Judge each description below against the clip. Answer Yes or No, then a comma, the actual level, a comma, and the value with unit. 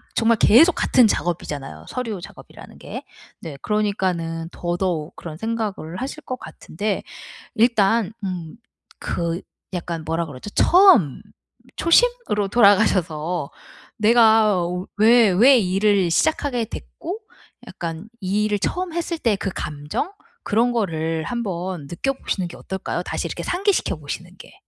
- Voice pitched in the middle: No, high, 200 Hz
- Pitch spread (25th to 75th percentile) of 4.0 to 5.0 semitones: No, wide, 5.5 semitones